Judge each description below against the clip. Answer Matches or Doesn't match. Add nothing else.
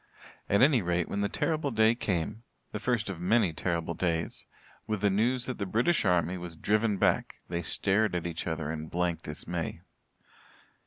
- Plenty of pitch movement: Doesn't match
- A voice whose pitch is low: Matches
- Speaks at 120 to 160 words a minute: Doesn't match